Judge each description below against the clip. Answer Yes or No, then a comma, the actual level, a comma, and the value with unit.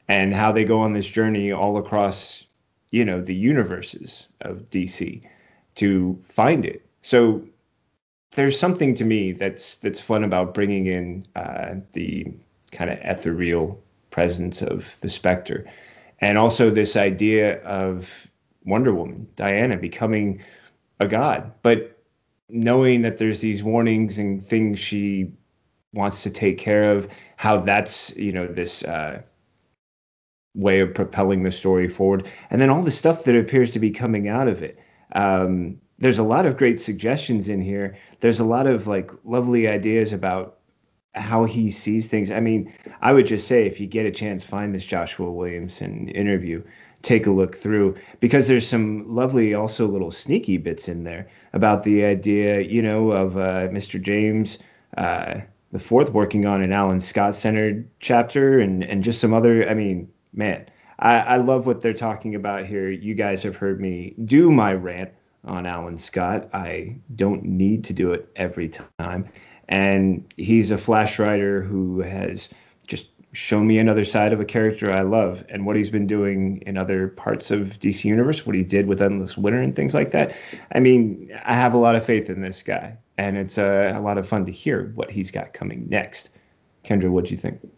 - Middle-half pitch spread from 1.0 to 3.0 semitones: Yes, average, 2.7 semitones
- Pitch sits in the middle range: No, low, 100 Hz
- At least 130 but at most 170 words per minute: No, average, 180 wpm